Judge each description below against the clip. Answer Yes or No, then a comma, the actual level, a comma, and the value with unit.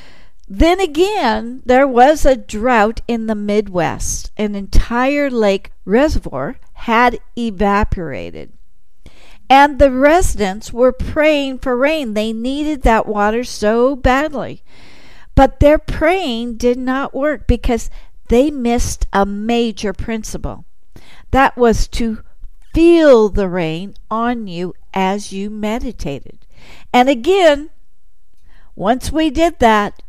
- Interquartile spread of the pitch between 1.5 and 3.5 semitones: No, average, 4.8 semitones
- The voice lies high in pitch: Yes, high, 240 Hz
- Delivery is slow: Yes, slow, 115 wpm